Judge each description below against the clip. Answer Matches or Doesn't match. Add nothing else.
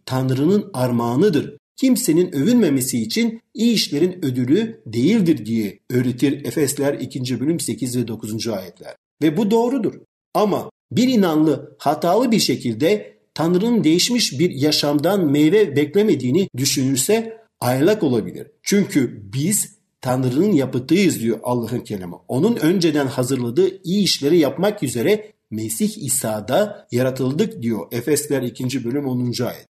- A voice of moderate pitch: Matches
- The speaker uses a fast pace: Doesn't match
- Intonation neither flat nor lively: Doesn't match